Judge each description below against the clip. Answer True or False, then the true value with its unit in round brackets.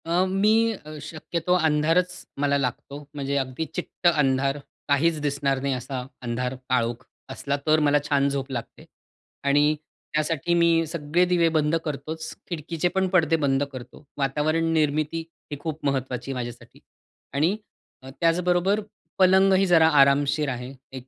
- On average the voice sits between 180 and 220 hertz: False (150 Hz)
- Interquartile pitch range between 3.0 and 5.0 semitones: True (3.5 semitones)